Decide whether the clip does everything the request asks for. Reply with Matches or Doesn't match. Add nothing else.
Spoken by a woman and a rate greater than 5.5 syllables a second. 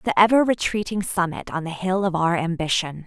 Doesn't match